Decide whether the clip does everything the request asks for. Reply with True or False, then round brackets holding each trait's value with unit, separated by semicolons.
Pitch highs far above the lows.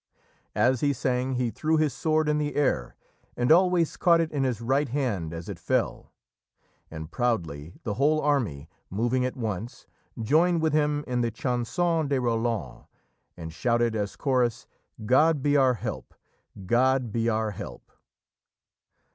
False (4.7 semitones)